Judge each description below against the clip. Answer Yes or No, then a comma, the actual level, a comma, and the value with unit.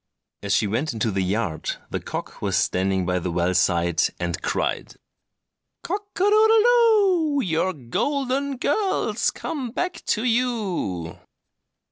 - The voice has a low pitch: No, high, 190 Hz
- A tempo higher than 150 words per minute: No, average, 140 wpm